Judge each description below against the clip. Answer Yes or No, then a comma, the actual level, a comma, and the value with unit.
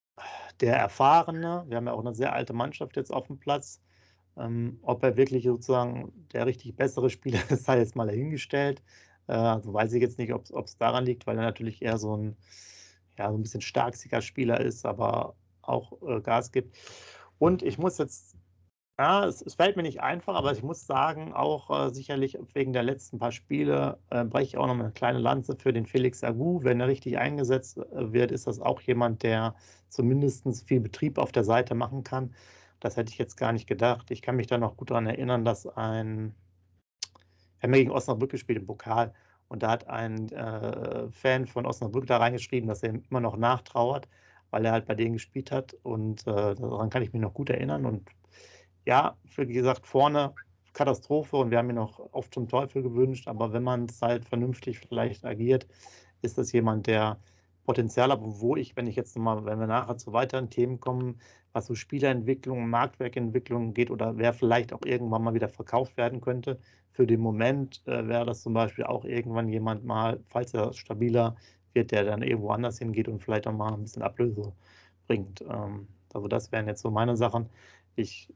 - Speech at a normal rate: No, fast, 200 wpm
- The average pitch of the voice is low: Yes, low, 120 Hz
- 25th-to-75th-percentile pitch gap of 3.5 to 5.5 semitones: No, narrow, 2.5 semitones